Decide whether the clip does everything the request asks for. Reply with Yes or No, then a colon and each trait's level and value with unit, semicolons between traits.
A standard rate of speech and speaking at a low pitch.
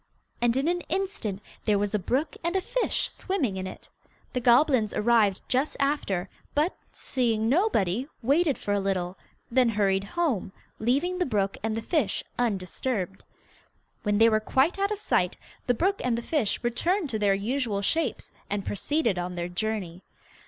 No: average, 170 wpm; high, 230 Hz